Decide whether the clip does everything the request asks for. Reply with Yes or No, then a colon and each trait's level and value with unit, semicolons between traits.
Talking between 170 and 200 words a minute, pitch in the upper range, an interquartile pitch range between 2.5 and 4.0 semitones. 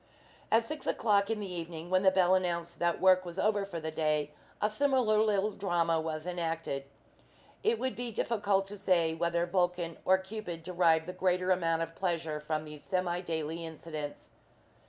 No: average, 175 wpm; medium, 175 Hz; average, 3.2 semitones